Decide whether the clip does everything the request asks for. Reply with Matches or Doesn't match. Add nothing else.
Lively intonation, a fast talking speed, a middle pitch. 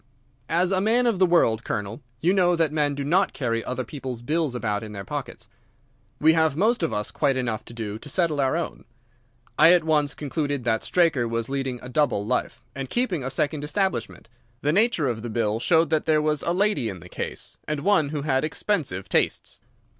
Matches